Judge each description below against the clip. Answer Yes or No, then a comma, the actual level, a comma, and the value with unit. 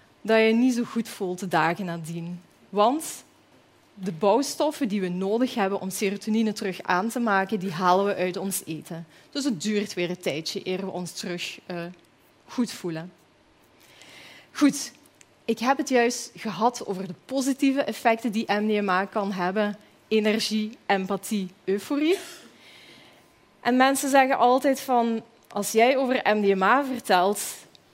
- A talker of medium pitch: No, high, 210 Hz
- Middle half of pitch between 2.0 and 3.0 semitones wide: No, average, 4.4 semitones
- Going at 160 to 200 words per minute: No, average, 150 wpm